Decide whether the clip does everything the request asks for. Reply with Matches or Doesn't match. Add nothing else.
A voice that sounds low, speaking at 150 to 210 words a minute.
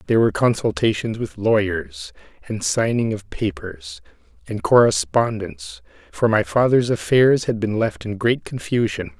Doesn't match